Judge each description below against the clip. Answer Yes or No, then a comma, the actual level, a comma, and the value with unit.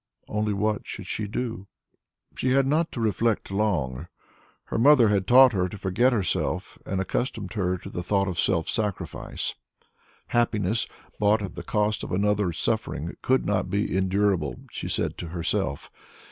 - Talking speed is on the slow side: No, average, 160 wpm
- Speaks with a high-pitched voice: No, low, 105 Hz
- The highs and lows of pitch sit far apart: No, average, 3.2 semitones